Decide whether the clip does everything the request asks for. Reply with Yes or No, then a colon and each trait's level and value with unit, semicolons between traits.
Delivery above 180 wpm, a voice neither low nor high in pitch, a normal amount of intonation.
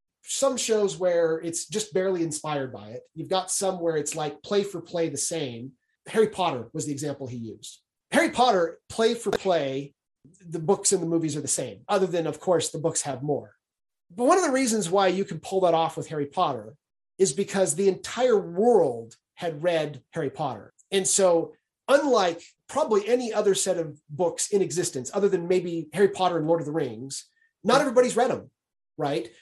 Yes: average, 200 wpm; medium, 175 Hz; average, 4.3 semitones